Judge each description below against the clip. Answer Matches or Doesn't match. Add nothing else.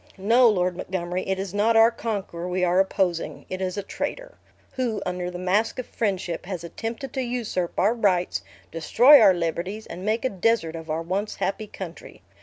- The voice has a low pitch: Doesn't match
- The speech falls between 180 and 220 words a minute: Matches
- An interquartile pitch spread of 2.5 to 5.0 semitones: Matches